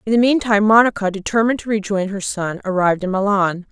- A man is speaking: No, female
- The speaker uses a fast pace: No, average, 195 wpm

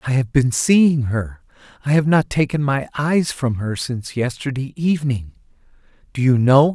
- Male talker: Yes, male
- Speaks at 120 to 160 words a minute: No, average, 170 wpm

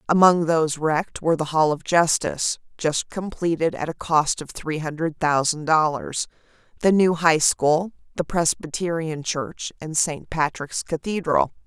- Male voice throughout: No, female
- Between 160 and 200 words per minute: No, average, 150 wpm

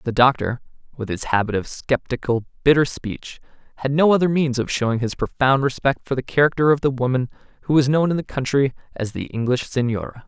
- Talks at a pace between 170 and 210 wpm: Yes, average, 200 wpm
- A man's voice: Yes, male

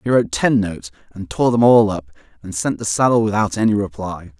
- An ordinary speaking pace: No, fast, 220 wpm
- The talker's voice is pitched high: No, low, 100 Hz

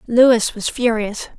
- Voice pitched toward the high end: Yes, high, 235 Hz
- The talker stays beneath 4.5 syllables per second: Yes, 3.5 syllables/s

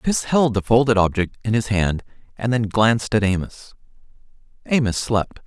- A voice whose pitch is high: No, low, 110 Hz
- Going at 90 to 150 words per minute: No, average, 165 wpm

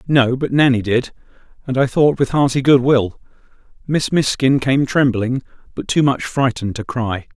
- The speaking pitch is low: Yes, low, 130 Hz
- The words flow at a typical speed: Yes, average, 170 wpm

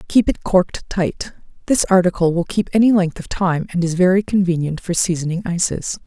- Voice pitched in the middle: Yes, medium, 180 Hz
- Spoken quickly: No, average, 190 wpm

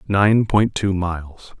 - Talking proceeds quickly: No, average, 150 wpm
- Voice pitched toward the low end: Yes, very low, 95 Hz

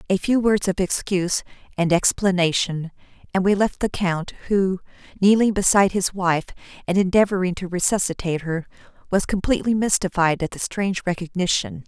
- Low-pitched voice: No, medium, 185 Hz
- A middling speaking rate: Yes, average, 145 wpm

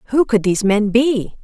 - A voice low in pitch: No, high, 225 Hz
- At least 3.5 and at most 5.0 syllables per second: No, 5.6 syllables/s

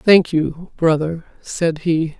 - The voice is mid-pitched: Yes, medium, 165 Hz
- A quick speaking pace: No, slow, 135 wpm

